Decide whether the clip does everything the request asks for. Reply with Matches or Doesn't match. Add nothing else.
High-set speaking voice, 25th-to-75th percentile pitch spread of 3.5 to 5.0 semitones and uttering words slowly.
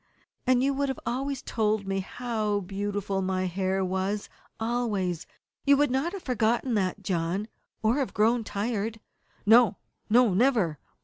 Doesn't match